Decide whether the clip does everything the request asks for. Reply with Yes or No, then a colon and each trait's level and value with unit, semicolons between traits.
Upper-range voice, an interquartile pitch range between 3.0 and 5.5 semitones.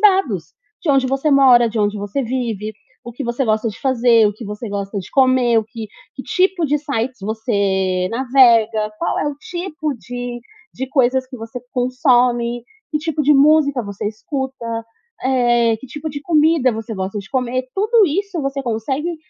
Yes: very high, 250 Hz; average, 4.0 semitones